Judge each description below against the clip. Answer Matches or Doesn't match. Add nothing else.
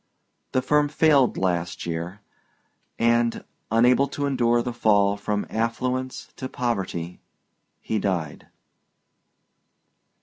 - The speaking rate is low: Matches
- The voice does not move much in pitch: Doesn't match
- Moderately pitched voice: Doesn't match